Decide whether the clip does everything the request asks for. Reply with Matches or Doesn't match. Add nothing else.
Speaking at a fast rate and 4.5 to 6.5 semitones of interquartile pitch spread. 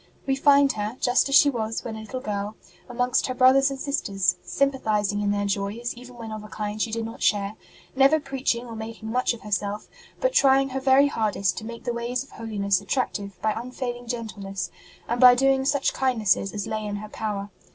Doesn't match